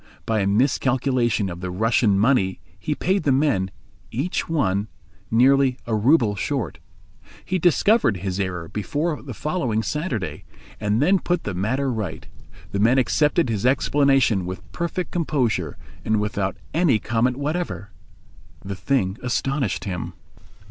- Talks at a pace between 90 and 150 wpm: Yes, average, 140 wpm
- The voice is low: Yes, low, 120 Hz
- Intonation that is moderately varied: No, wide, 6.1 semitones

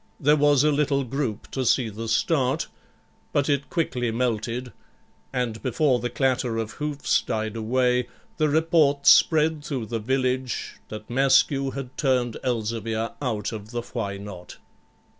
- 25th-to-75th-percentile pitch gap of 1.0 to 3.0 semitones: No, average, 3.7 semitones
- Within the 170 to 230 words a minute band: No, average, 145 wpm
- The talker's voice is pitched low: Yes, low, 125 Hz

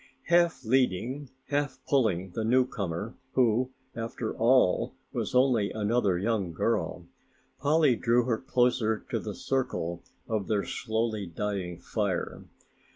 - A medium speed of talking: No, slow, 120 wpm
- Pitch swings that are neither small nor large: Yes, average, 4.1 semitones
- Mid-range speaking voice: No, low, 115 Hz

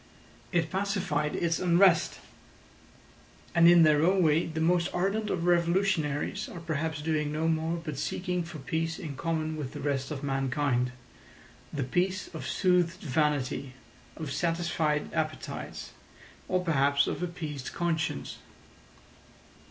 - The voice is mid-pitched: Yes, medium, 160 Hz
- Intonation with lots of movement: No, average, 2.8 semitones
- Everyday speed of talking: No, slow, 130 wpm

